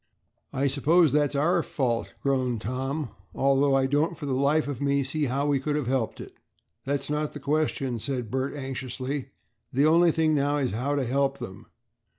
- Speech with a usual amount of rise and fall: No, narrow, 2.0 semitones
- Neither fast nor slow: Yes, average, 185 wpm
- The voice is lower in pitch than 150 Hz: Yes, medium, 140 Hz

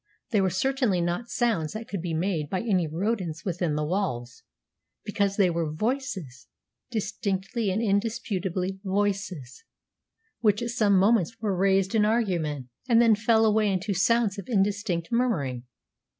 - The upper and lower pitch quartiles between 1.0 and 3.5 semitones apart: No, average, 4.1 semitones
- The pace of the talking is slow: No, average, 150 wpm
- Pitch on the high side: Yes, high, 195 Hz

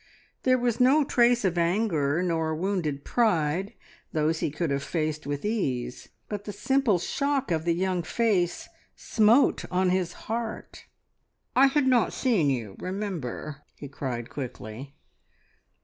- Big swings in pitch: Yes, wide, 7.1 semitones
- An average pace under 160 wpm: Yes, average, 140 wpm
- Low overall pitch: No, medium, 180 Hz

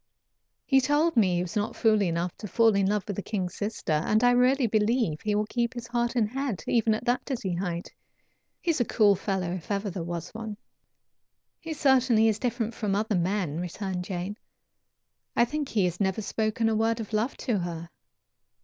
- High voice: Yes, high, 215 Hz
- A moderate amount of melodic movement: Yes, average, 4.2 semitones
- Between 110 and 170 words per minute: No, fast, 205 wpm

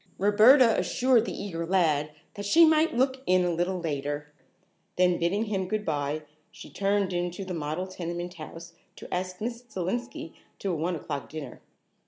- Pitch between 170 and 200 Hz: Yes, medium, 185 Hz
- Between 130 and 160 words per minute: No, average, 175 wpm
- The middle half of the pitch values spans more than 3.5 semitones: Yes, average, 3.9 semitones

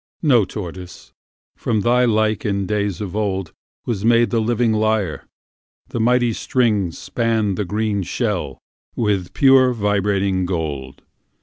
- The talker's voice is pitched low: Yes, low, 105 Hz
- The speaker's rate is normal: No, slow, 120 wpm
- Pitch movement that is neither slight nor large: Yes, average, 3.3 semitones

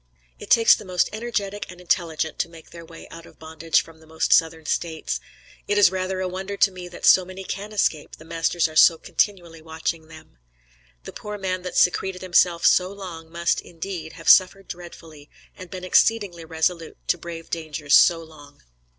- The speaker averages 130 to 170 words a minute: No, average, 190 wpm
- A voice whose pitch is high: No, medium, 170 Hz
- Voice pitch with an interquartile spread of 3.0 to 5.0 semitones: No, narrow, 2.5 semitones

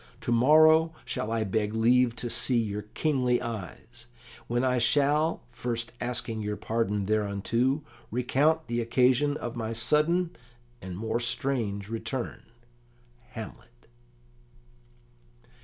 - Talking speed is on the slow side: Yes, slow, 115 wpm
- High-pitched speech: No, low, 120 Hz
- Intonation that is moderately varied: Yes, average, 3.1 semitones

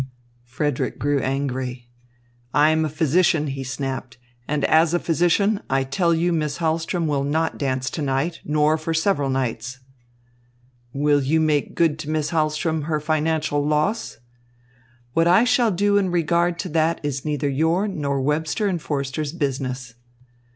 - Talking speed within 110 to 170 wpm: Yes, average, 155 wpm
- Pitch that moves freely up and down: No, average, 3.1 semitones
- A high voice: No, medium, 155 Hz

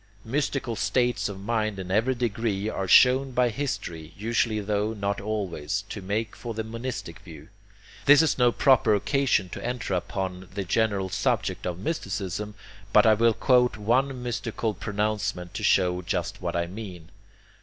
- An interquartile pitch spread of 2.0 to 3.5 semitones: No, average, 3.9 semitones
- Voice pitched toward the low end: Yes, low, 105 Hz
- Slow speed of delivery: No, average, 160 wpm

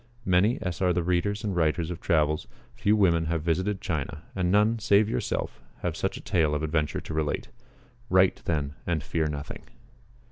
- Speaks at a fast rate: No, average, 180 wpm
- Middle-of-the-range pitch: No, very low, 85 Hz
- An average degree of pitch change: Yes, average, 3.6 semitones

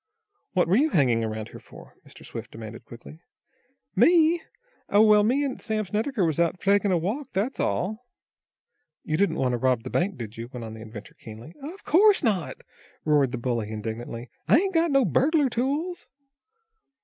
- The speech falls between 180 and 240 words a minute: Yes, average, 185 wpm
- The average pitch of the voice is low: No, medium, 185 Hz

